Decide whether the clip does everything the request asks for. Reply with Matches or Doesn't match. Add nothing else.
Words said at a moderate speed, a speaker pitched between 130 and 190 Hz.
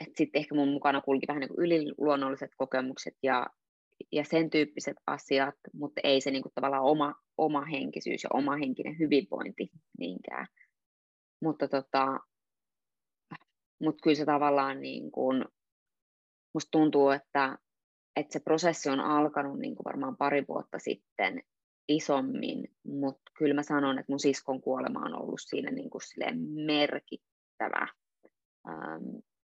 Matches